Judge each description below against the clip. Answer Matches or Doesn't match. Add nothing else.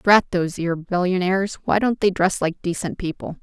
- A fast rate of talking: Doesn't match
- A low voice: Doesn't match